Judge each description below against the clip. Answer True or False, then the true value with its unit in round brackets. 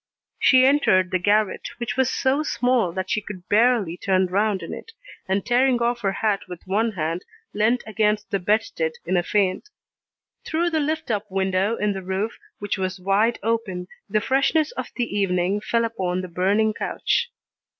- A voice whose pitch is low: False (210 Hz)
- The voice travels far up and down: False (4.0 semitones)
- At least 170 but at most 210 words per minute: True (180 wpm)